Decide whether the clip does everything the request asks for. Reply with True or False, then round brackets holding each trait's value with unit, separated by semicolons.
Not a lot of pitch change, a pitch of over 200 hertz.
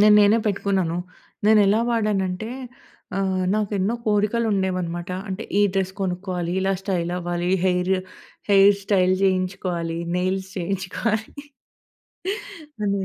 False (2.0 semitones; 190 Hz)